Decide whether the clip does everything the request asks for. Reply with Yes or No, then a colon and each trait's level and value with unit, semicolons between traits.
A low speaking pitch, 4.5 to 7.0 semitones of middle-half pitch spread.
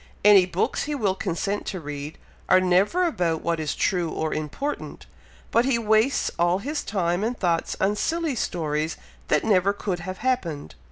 No: medium, 185 Hz; average, 4.8 semitones